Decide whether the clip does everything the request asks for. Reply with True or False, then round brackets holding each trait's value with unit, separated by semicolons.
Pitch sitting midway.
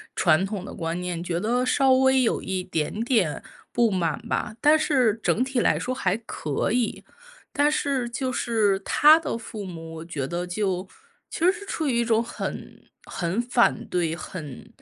False (220 Hz)